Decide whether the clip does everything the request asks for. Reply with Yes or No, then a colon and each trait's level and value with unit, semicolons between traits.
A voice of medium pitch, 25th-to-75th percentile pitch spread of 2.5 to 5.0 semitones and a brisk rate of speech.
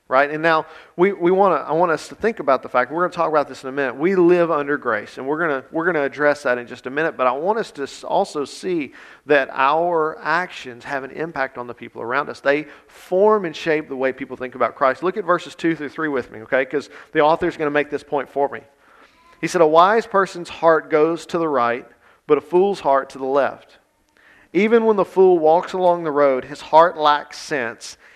Yes: medium, 155 Hz; average, 4.1 semitones; fast, 245 wpm